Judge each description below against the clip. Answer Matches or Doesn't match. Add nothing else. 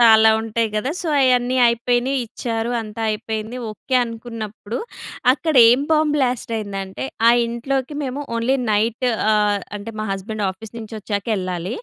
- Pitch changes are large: Doesn't match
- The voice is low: Doesn't match